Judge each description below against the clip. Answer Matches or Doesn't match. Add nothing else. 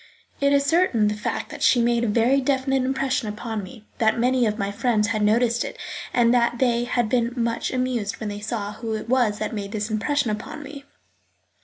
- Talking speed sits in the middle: Doesn't match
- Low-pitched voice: Doesn't match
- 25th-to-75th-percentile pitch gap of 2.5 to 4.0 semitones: Matches